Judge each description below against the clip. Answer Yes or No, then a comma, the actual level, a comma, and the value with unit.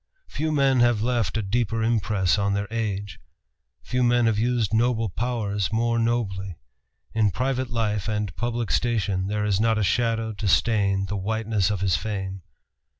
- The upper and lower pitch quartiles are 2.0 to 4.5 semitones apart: Yes, average, 2.8 semitones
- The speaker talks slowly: No, average, 165 wpm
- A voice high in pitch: No, low, 110 Hz